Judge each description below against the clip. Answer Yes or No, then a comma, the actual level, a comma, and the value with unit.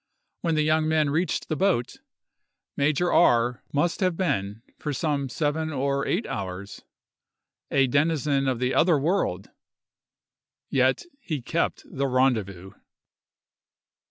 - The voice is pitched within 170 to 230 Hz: No, medium, 140 Hz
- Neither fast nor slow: No, slow, 125 wpm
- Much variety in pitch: No, average, 4.1 semitones